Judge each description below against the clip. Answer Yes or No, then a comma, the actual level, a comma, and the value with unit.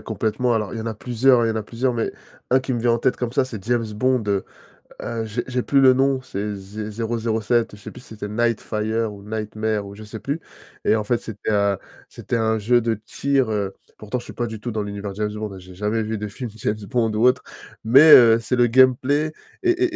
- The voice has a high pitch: No, low, 115 Hz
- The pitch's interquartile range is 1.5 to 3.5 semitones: Yes, average, 2.7 semitones